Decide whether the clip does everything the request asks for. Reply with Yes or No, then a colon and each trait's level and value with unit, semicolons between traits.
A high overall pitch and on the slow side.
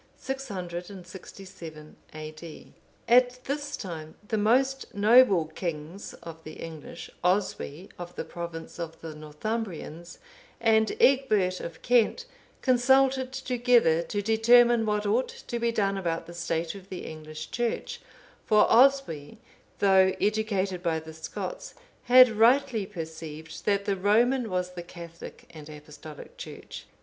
Yes: high, 195 Hz; slow, 130 wpm